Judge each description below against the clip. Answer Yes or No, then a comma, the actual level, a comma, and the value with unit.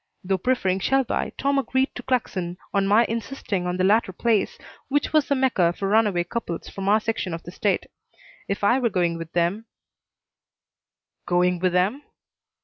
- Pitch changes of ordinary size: Yes, average, 4.7 semitones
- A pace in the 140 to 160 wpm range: No, average, 170 wpm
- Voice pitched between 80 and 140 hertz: No, high, 200 Hz